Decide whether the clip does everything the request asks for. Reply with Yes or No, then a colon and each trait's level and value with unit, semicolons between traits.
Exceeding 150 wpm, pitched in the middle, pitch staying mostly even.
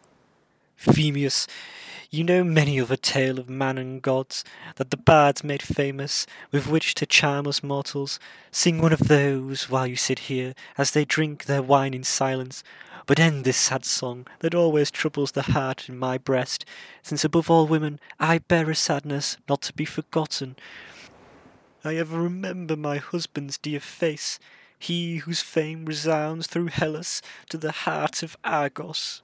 No: average, 165 wpm; medium, 145 Hz; average, 3.0 semitones